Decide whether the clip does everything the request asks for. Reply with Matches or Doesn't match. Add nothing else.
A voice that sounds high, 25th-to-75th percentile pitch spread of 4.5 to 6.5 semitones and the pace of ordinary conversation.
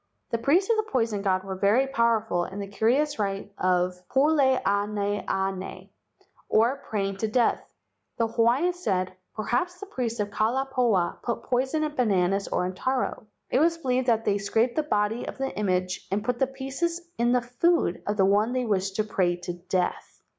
Matches